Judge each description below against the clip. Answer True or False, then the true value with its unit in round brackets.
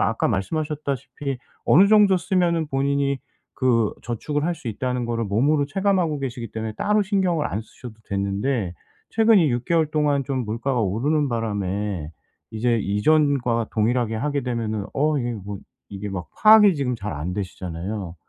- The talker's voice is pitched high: False (125 Hz)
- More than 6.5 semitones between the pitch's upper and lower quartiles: False (6.0 semitones)